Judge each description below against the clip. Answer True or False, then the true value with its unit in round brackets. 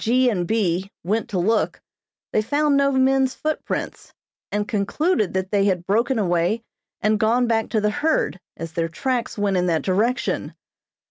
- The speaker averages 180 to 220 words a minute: False (170 wpm)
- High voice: True (215 Hz)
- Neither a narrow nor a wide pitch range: True (5.0 semitones)